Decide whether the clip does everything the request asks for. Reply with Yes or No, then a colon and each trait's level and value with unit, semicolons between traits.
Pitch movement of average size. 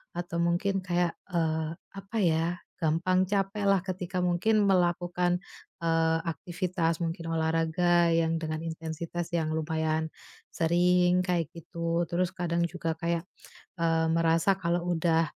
No: narrow, 1.6 semitones